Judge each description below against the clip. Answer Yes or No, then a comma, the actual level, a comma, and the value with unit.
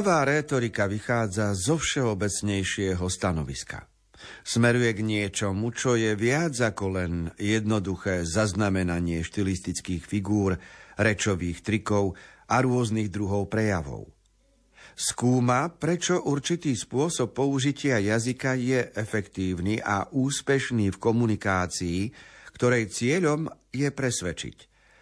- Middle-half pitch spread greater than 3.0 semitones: Yes, average, 4.5 semitones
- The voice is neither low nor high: No, low, 110 Hz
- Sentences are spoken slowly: Yes, slow, 95 wpm